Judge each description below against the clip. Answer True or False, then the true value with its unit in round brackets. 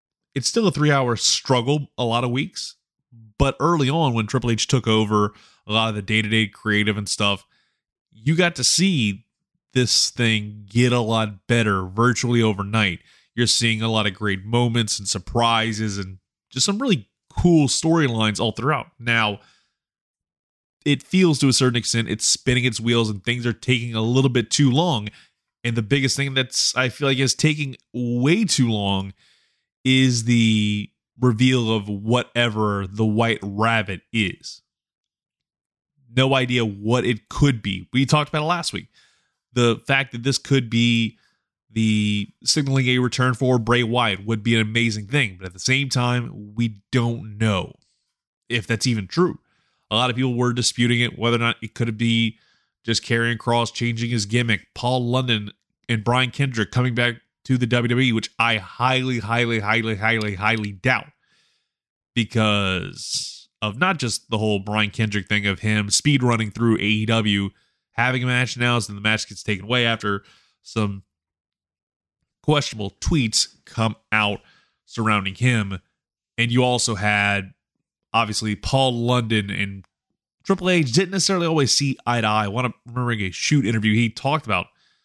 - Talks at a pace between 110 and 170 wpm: True (165 wpm)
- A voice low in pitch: True (115 Hz)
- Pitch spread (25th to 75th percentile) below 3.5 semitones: True (3.0 semitones)